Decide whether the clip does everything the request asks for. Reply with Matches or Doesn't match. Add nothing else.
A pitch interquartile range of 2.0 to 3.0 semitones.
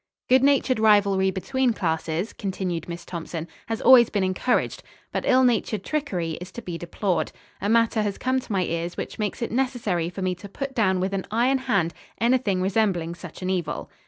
Doesn't match